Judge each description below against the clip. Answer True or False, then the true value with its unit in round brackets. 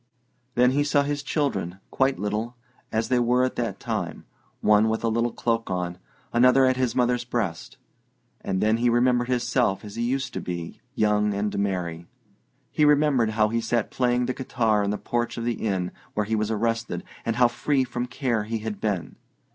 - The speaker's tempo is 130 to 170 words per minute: False (195 wpm)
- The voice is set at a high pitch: False (115 Hz)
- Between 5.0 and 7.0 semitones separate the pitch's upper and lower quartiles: False (3.0 semitones)